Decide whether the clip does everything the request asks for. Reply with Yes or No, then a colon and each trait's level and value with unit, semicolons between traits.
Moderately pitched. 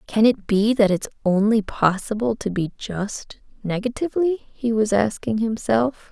No: high, 220 Hz